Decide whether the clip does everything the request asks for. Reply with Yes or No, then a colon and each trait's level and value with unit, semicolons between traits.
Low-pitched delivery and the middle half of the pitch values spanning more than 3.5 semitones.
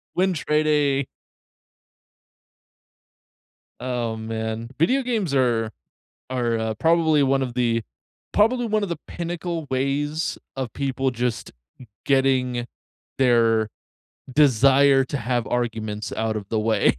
Yes: low, 130 Hz; average, 4.7 semitones